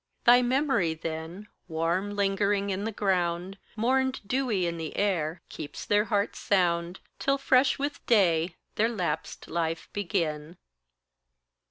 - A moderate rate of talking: No, slow, 130 wpm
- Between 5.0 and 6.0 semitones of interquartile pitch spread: No, average, 4.3 semitones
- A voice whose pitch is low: No, high, 195 Hz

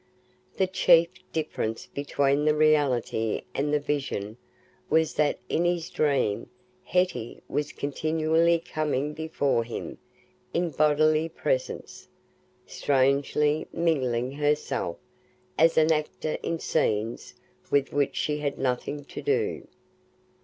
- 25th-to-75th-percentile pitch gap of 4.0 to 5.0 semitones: No, narrow, 2.6 semitones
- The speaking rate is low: Yes, slow, 110 wpm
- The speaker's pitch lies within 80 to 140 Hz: No, medium, 150 Hz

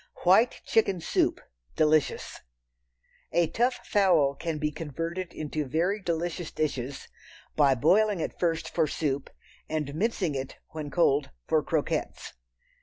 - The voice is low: No, medium, 160 Hz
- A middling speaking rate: No, slow, 125 wpm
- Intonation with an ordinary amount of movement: Yes, average, 3.4 semitones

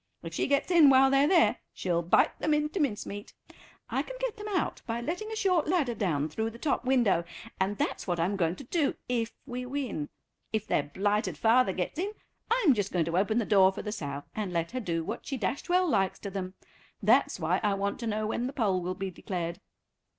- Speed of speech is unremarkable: No, fast, 225 wpm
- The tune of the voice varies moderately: No, wide, 7.0 semitones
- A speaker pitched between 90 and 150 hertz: No, high, 220 Hz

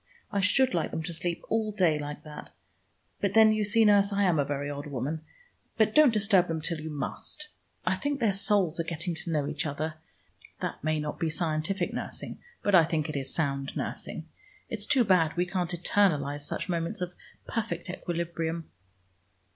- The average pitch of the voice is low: No, medium, 170 Hz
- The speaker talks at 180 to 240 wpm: Yes, average, 190 wpm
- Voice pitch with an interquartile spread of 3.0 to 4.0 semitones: No, average, 4.7 semitones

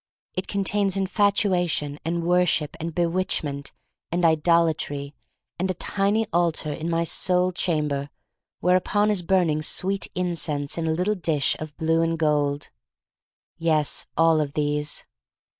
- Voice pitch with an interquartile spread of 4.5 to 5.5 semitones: No, average, 3.2 semitones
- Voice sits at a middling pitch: Yes, medium, 165 Hz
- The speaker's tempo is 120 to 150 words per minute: Yes, average, 140 wpm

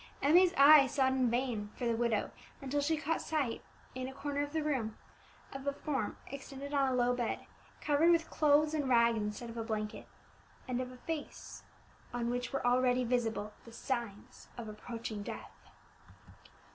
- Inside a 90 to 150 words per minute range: No, average, 175 wpm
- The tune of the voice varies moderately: Yes, average, 3.6 semitones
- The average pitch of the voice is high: Yes, very high, 255 Hz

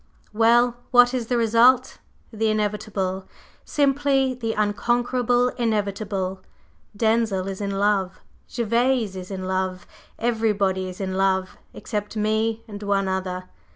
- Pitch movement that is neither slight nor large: Yes, average, 3.6 semitones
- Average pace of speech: No, slow, 120 wpm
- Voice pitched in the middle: No, high, 215 Hz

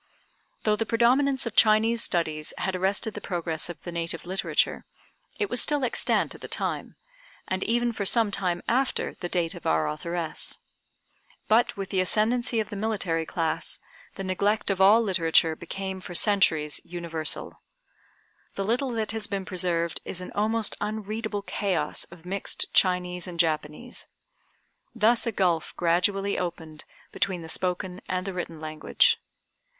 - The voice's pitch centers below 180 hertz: No, high, 190 Hz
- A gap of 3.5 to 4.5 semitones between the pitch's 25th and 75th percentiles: Yes, average, 4.1 semitones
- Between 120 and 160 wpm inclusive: Yes, average, 155 wpm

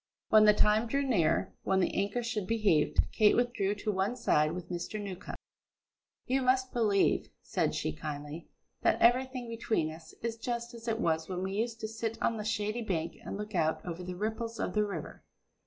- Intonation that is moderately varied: Yes, average, 4.3 semitones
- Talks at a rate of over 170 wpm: Yes, average, 200 wpm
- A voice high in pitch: Yes, high, 210 Hz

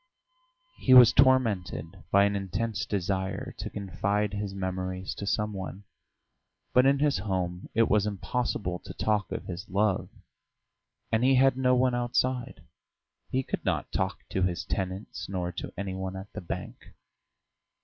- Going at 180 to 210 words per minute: No, average, 155 wpm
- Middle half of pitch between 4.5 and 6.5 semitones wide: No, average, 3.9 semitones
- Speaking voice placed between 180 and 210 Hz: No, low, 100 Hz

